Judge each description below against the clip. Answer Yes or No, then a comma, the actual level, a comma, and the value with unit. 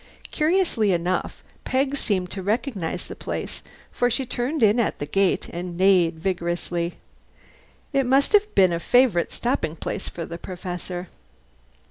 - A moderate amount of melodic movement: No, wide, 6.2 semitones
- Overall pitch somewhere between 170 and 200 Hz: Yes, high, 190 Hz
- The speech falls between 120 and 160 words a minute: Yes, average, 145 wpm